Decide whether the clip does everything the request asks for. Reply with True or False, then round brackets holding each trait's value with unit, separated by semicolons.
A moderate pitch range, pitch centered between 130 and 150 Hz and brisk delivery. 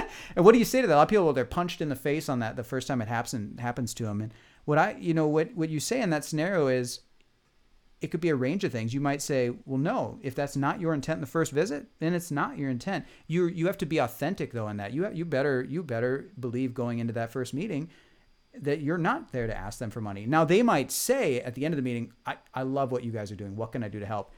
True (4.7 semitones; 135 Hz; 295 wpm)